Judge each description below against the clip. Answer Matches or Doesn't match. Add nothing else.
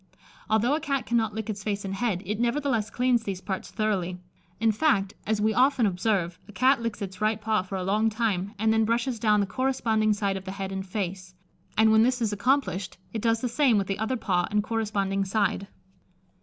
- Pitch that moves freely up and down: Doesn't match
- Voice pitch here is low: Doesn't match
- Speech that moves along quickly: Matches